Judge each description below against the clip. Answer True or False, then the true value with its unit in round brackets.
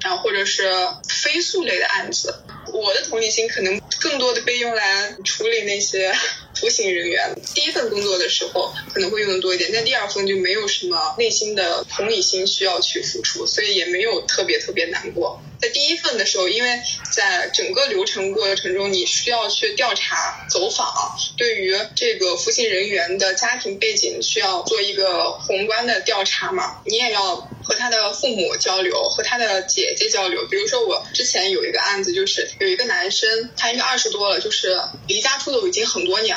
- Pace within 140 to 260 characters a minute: False (300 characters per minute)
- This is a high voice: True (360 Hz)